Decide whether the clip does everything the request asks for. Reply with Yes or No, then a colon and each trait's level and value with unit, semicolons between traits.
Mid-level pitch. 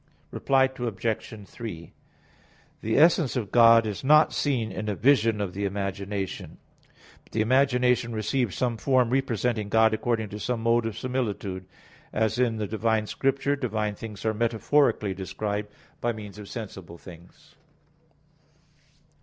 No: low, 110 Hz